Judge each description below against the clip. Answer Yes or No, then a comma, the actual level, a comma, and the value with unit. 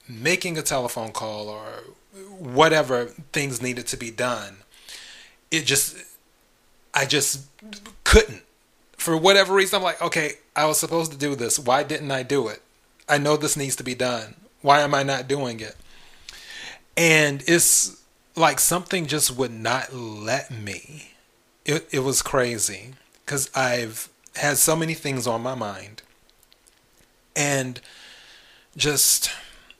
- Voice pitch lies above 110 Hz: Yes, medium, 140 Hz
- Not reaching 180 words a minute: Yes, average, 140 wpm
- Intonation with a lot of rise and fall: No, average, 4.2 semitones